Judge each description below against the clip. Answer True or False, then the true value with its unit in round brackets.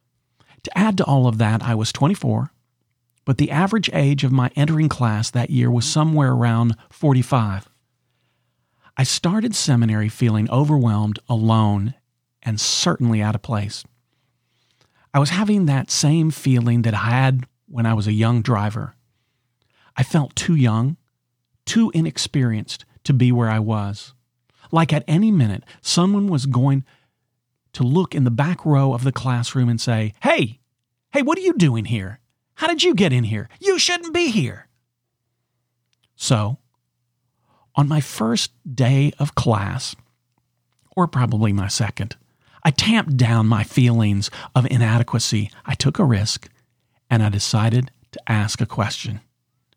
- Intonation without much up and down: False (3.0 semitones)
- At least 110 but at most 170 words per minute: True (150 wpm)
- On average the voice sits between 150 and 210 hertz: False (125 Hz)